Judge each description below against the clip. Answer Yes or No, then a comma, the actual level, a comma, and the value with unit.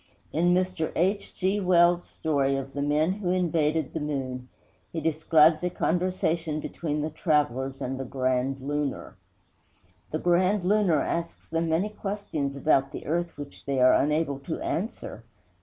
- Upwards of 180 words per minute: No, average, 155 wpm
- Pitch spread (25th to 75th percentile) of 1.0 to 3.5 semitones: No, average, 3.9 semitones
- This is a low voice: No, medium, 155 Hz